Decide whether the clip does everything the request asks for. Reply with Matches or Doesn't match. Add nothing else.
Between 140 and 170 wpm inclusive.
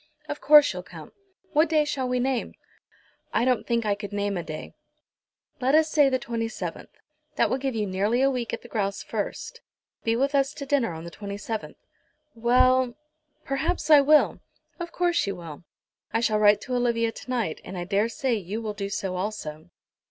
Doesn't match